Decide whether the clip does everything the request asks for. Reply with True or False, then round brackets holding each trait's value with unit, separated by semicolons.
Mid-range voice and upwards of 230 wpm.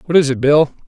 True (145 Hz; 275 wpm)